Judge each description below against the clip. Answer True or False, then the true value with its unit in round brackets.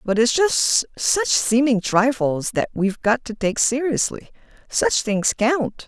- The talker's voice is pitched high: True (240 Hz)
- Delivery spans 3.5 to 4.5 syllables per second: True (3.9 syllables/s)